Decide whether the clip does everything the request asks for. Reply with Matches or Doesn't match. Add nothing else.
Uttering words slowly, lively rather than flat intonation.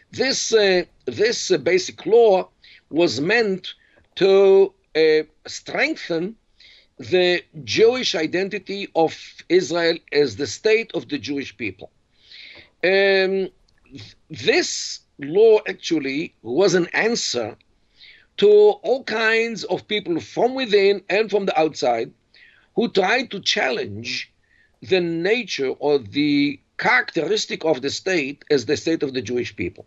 Matches